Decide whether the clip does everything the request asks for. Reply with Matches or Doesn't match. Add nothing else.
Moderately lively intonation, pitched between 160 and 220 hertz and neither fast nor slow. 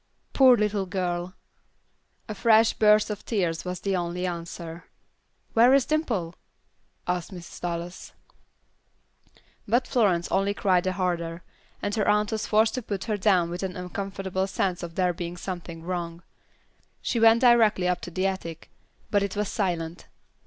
Matches